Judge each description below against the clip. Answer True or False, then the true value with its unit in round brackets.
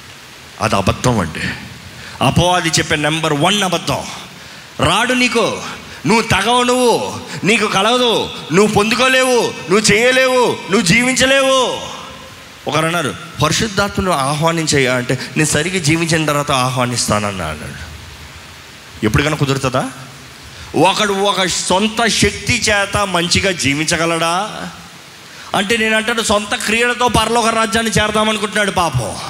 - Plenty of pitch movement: True (8.3 semitones)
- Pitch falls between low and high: True (175 Hz)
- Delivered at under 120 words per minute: True (100 wpm)